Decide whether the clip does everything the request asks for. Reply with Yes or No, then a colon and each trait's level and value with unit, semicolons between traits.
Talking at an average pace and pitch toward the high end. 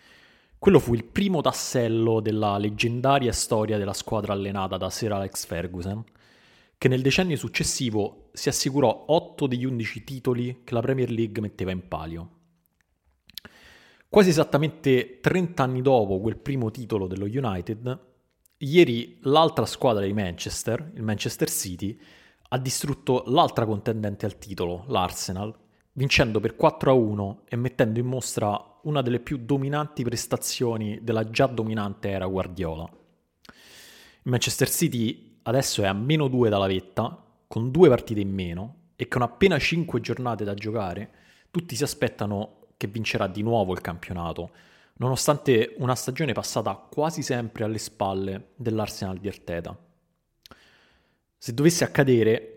No: average, 135 wpm; low, 115 Hz